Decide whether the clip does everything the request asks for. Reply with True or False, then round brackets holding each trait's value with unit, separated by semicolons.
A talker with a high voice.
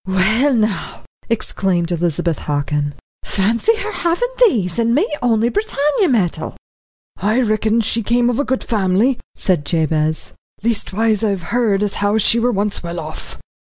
True (215 Hz)